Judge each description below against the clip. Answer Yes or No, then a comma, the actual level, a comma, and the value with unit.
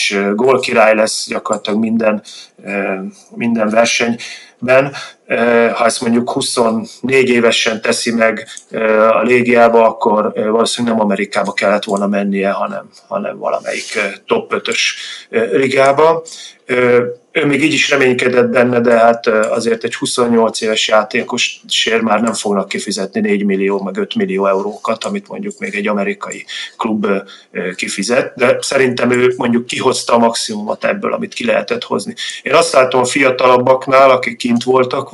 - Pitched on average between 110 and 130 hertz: Yes, low, 120 Hz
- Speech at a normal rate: Yes, average, 135 wpm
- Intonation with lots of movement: No, average, 2.7 semitones